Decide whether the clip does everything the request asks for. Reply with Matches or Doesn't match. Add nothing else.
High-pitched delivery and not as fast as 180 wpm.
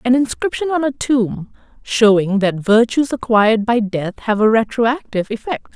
Matches